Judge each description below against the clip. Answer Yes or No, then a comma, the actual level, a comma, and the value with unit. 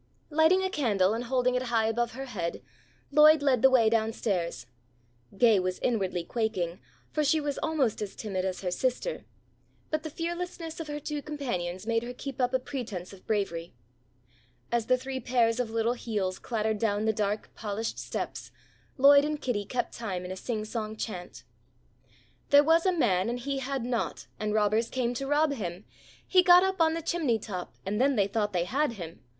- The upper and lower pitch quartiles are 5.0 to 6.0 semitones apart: Yes, average, 5.3 semitones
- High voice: Yes, high, 235 Hz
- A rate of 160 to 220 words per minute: Yes, average, 190 wpm